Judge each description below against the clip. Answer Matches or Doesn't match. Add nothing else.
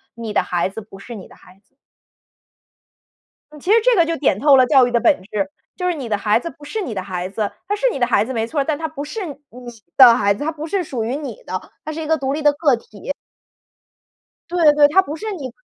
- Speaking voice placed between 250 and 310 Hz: Matches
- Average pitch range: Doesn't match